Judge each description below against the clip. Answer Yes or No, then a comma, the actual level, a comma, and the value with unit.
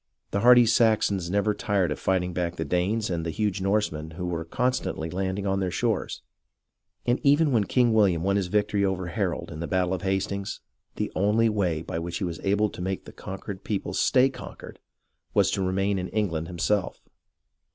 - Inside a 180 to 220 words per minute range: Yes, average, 195 wpm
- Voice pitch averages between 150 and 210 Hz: No, very low, 95 Hz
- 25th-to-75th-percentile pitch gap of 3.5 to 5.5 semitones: No, average, 3.0 semitones